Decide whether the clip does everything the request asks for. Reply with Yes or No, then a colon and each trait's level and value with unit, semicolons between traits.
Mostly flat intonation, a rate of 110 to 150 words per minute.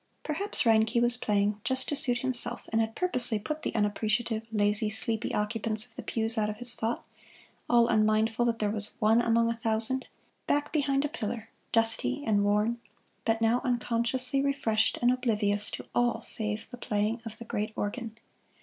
No: narrow, 2.1 semitones; average, 175 wpm